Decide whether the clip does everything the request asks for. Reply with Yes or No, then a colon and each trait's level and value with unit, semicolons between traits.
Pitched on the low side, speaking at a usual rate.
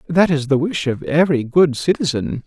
No: medium, 150 Hz; average, 195 wpm